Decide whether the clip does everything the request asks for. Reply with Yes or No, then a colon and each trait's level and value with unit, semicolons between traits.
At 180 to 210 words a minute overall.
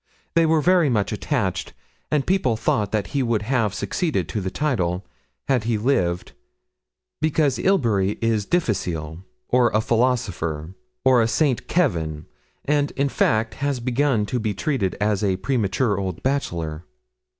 No: average, 150 wpm